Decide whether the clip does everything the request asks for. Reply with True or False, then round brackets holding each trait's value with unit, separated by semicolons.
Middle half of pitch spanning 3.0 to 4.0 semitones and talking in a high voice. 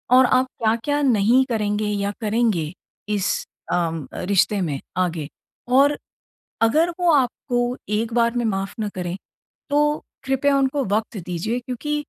False (4.7 semitones; 230 Hz)